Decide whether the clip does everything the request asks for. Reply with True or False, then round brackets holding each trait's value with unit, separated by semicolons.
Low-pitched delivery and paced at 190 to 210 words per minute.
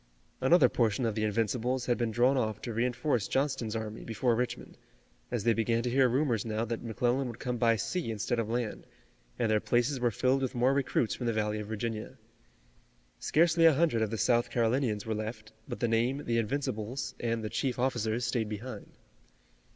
True (120 Hz; 195 wpm)